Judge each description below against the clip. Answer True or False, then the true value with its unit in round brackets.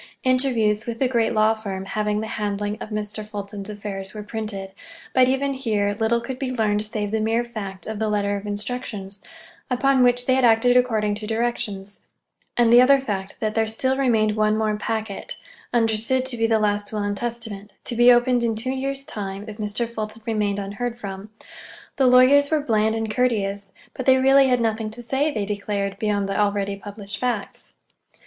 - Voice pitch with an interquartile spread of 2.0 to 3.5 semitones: True (3.0 semitones)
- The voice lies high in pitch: True (220 Hz)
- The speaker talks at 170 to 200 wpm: True (190 wpm)